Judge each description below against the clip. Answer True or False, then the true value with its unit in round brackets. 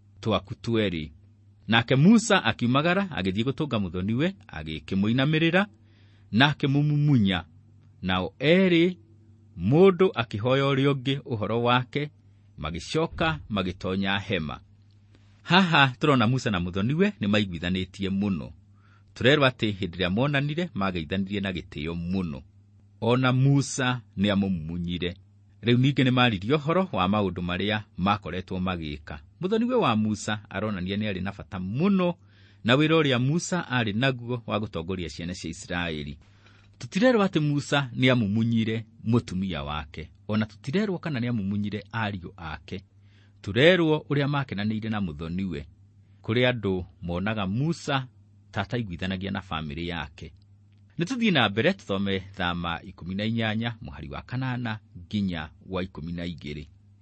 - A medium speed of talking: False (110 wpm)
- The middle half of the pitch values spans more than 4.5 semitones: True (5.2 semitones)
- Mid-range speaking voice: False (105 Hz)